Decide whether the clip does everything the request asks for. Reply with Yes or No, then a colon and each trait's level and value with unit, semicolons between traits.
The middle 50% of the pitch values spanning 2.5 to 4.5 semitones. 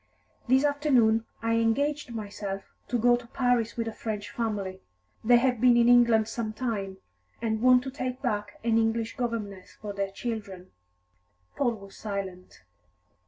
Yes: average, 2.9 semitones